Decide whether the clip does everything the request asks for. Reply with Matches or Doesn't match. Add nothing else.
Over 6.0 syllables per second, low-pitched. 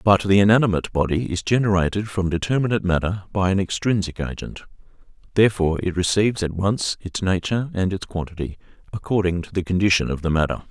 Matches